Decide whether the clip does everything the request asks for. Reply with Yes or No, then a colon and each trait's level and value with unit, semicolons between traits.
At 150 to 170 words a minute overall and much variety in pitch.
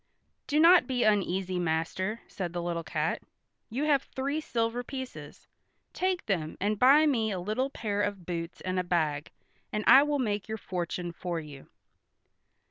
Yes: average, 165 wpm; wide, 6.8 semitones